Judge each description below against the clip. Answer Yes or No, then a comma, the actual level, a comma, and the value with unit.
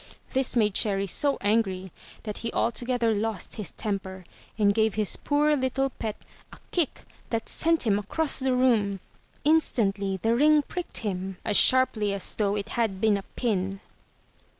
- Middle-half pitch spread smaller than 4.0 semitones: No, average, 4.4 semitones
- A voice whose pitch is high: Yes, high, 220 Hz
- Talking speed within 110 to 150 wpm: No, average, 160 wpm